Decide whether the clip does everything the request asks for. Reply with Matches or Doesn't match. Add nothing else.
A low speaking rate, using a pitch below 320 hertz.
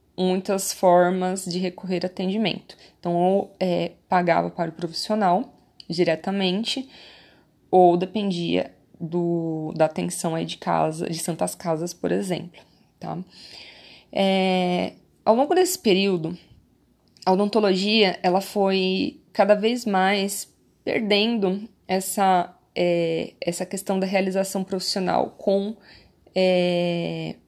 Matches